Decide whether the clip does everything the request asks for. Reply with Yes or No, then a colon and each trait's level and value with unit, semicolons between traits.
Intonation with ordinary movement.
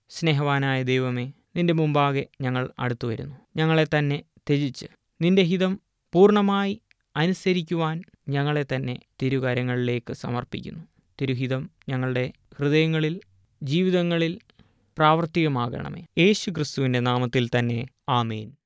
Yes: average, 4.9 semitones